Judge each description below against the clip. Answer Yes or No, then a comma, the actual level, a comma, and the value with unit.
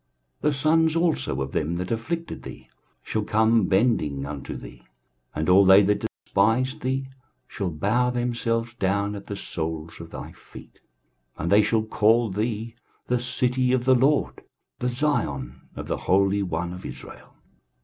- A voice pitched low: Yes, low, 110 Hz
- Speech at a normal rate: Yes, average, 160 wpm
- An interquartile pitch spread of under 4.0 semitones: No, wide, 5.4 semitones